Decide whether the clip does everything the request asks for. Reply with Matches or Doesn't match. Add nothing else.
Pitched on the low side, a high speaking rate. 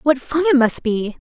Doesn't match